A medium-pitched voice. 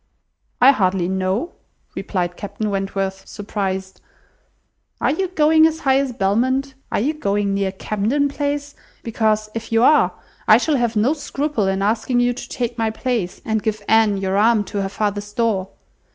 No: high, 220 Hz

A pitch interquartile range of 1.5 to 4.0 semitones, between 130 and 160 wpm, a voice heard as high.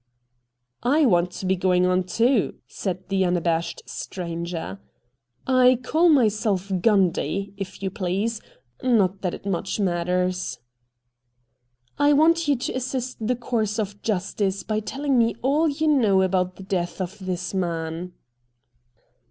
No: average, 4.9 semitones; average, 150 wpm; high, 195 Hz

